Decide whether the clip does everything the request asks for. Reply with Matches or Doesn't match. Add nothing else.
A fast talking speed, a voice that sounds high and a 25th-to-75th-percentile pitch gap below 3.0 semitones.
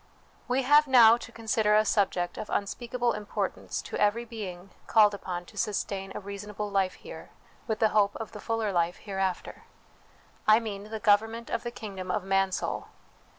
Doesn't match